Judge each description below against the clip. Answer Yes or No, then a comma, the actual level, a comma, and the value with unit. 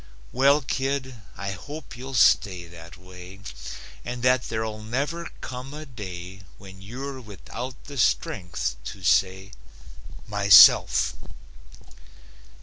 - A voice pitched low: Yes, low, 110 Hz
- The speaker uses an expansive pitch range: Yes, wide, 5.8 semitones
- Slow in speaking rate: Yes, slow, 110 wpm